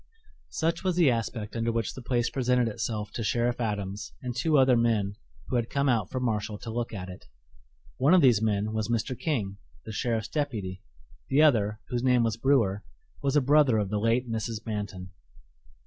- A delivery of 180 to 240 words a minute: Yes, average, 195 wpm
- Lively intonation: No, average, 3.3 semitones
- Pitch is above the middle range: No, low, 115 Hz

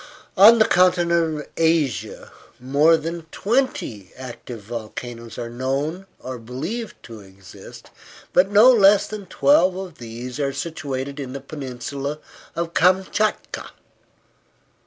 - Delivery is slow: Yes, slow, 120 wpm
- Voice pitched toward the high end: No, medium, 150 Hz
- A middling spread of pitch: No, wide, 6.5 semitones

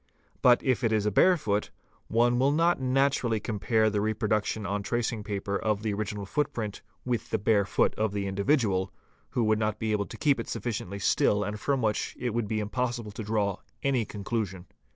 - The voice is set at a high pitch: No, low, 110 Hz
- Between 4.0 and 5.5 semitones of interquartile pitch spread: No, average, 2.8 semitones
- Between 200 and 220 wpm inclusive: Yes, fast, 205 wpm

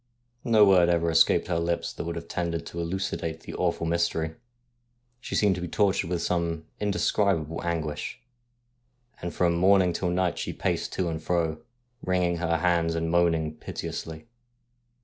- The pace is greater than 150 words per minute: Yes, average, 165 wpm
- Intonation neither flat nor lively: No, narrow, 1.5 semitones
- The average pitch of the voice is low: Yes, very low, 85 Hz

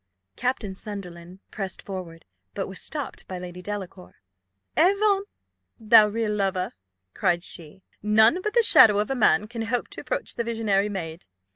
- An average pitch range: Yes, average, 4.0 semitones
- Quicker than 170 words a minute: No, average, 155 wpm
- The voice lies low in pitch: No, high, 205 Hz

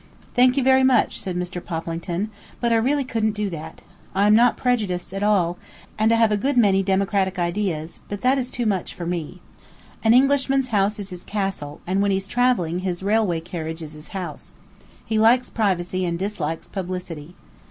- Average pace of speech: Yes, average, 190 wpm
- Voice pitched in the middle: No, high, 195 Hz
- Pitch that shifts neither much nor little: Yes, average, 4.2 semitones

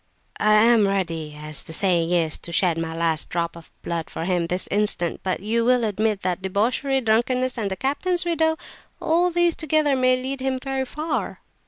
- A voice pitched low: No, high, 215 Hz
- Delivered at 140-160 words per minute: No, average, 190 wpm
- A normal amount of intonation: No, wide, 7.5 semitones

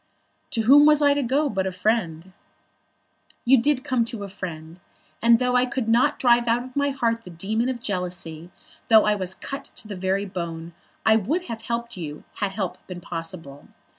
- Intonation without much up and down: No, wide, 5.5 semitones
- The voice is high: Yes, high, 220 Hz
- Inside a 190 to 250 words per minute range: Yes, average, 200 wpm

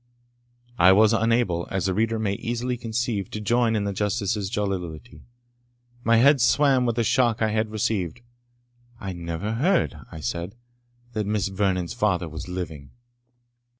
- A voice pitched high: No, low, 105 Hz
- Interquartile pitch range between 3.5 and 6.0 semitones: Yes, average, 3.9 semitones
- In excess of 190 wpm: No, average, 150 wpm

